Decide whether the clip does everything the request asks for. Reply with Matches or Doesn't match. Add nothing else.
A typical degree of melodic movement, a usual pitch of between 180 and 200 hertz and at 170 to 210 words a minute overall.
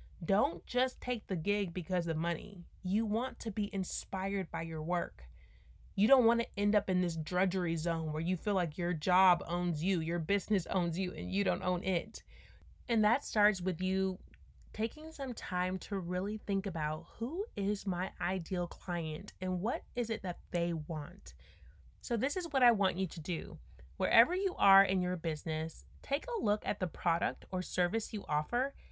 Matches